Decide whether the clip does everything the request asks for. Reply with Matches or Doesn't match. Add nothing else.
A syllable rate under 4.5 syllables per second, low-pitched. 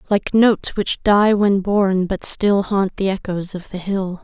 Doesn't match